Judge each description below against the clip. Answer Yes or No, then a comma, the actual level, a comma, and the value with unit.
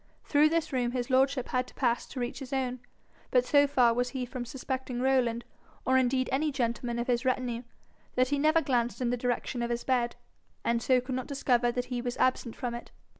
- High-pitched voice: Yes, very high, 250 Hz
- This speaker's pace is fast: Yes, fast, 220 wpm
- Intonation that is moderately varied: No, narrow, 1.5 semitones